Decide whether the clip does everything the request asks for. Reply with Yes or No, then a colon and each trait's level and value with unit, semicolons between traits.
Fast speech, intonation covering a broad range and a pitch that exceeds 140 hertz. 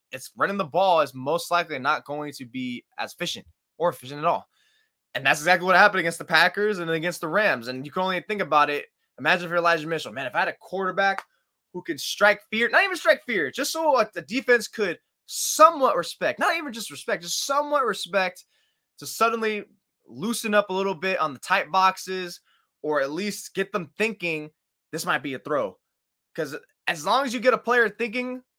Yes: fast, 210 wpm; wide, 5.8 semitones; high, 190 Hz